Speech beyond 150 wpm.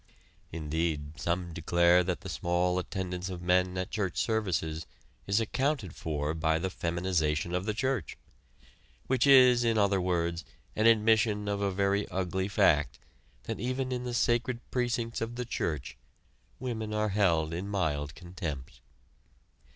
No: average, 145 wpm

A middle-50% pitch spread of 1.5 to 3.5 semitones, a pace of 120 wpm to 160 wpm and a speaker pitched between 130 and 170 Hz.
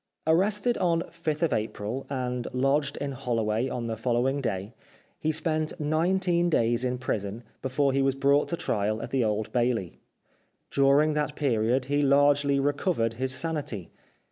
No: average, 4.1 semitones; average, 150 wpm; low, 135 Hz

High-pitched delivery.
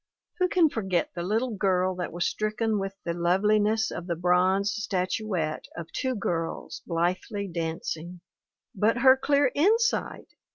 Yes: high, 195 Hz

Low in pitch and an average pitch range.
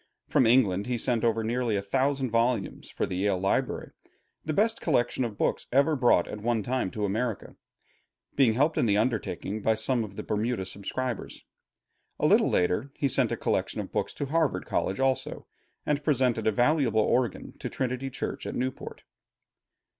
Yes: low, 120 Hz; average, 3.6 semitones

